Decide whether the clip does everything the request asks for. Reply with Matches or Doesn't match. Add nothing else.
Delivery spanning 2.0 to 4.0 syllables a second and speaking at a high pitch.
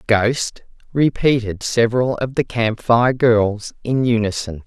Doesn't match